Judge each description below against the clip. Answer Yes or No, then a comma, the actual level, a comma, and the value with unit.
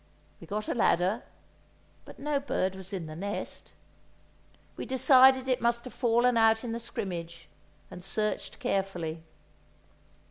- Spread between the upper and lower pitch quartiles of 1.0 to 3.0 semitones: No, average, 4.8 semitones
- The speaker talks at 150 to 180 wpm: No, average, 140 wpm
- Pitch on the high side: Yes, high, 220 Hz